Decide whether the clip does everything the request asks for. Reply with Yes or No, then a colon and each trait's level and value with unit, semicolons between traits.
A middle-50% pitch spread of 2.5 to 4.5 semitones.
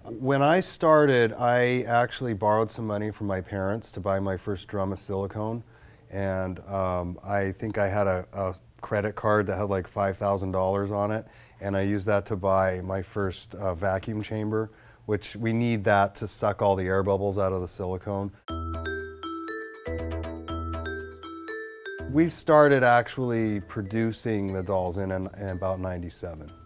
Yes: average, 2.9 semitones